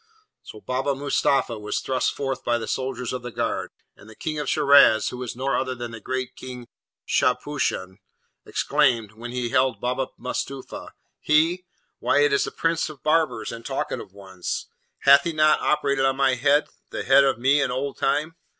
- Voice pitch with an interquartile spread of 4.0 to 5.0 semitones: No, average, 2.8 semitones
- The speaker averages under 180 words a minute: No, average, 185 wpm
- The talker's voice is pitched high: No, low, 130 Hz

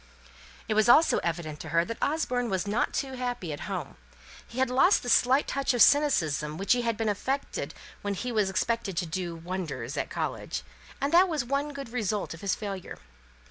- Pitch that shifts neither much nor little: No, wide, 6.3 semitones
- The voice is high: Yes, high, 225 Hz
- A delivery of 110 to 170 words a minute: No, average, 195 wpm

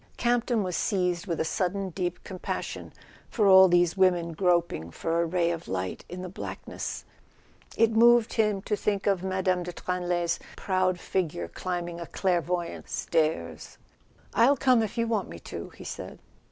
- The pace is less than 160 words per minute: No, average, 165 wpm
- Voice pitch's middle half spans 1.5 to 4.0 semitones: Yes, narrow, 2.6 semitones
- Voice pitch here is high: No, medium, 180 Hz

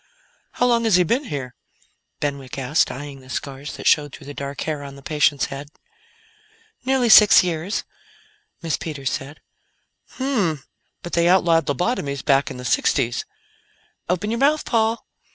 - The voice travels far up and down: Yes, wide, 7.1 semitones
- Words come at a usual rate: Yes, average, 155 wpm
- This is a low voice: No, medium, 150 Hz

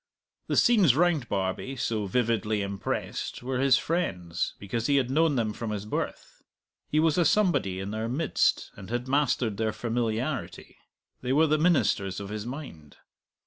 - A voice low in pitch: Yes, low, 120 Hz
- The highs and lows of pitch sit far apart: Yes, wide, 5.8 semitones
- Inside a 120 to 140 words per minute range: No, average, 165 wpm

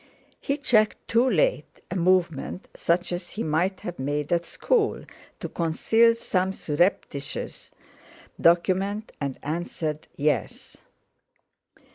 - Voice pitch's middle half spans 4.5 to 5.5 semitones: Yes, average, 5.1 semitones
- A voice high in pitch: No, medium, 175 Hz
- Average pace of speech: No, slow, 110 wpm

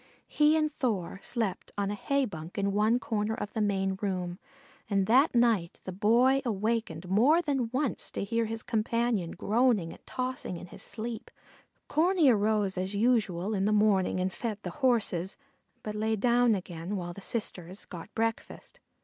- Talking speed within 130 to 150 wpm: No, average, 170 wpm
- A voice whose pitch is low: No, high, 215 Hz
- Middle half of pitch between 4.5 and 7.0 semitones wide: No, average, 3.9 semitones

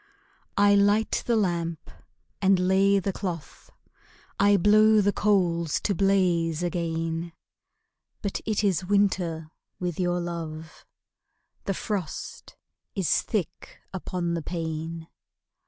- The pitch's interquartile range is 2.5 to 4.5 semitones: Yes, average, 3.2 semitones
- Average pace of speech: No, slow, 110 wpm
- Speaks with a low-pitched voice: No, medium, 180 Hz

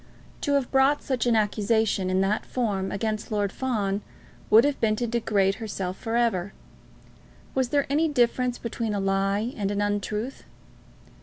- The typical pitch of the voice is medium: No, high, 220 Hz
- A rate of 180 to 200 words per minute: No, average, 160 wpm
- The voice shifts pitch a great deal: No, average, 3.6 semitones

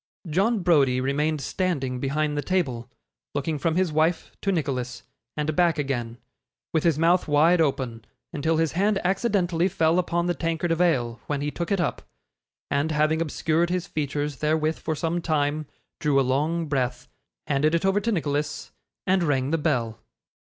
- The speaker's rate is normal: Yes, average, 170 wpm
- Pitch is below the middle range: No, medium, 155 Hz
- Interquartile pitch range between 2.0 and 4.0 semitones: Yes, average, 3.4 semitones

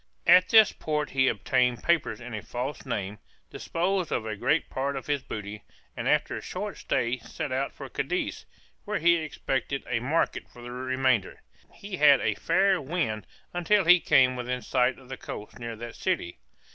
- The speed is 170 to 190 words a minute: Yes, average, 185 wpm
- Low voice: Yes, low, 130 Hz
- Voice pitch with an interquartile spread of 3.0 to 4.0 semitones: No, average, 5.3 semitones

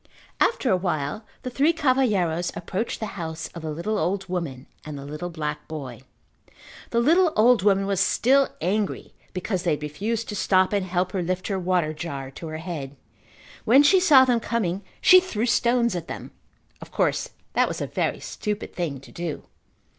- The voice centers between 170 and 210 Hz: Yes, medium, 185 Hz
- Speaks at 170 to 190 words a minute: Yes, average, 185 wpm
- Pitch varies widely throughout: Yes, wide, 6.2 semitones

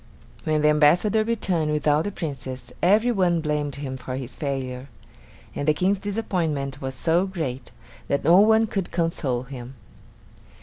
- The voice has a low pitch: No, medium, 150 Hz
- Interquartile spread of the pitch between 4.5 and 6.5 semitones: Yes, wide, 5.5 semitones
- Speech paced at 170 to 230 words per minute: No, average, 150 wpm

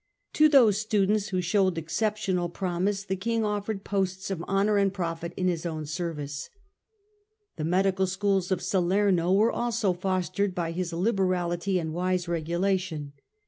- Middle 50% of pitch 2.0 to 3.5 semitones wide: Yes, narrow, 2.6 semitones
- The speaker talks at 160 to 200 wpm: No, average, 145 wpm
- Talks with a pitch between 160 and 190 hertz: Yes, medium, 185 Hz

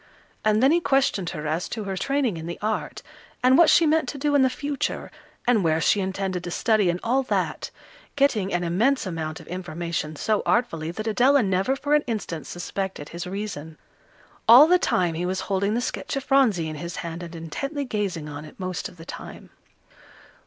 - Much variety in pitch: Yes, wide, 7.0 semitones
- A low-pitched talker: No, high, 195 Hz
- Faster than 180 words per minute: Yes, average, 200 wpm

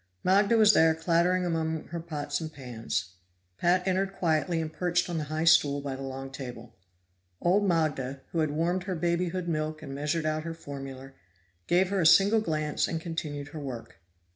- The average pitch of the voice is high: No, medium, 160 Hz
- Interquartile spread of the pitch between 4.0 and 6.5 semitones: No, average, 3.4 semitones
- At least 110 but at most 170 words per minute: No, average, 185 wpm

